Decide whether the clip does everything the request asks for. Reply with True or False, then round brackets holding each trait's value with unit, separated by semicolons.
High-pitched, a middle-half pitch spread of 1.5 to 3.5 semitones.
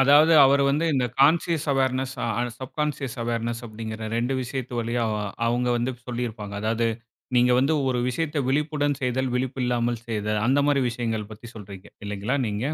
False (125 Hz; 3.0 semitones)